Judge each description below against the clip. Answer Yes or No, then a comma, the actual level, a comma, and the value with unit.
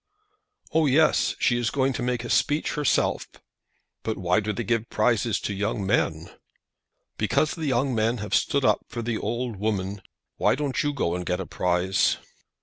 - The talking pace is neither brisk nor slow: Yes, average, 180 wpm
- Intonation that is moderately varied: Yes, average, 4.5 semitones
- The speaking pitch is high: No, low, 115 Hz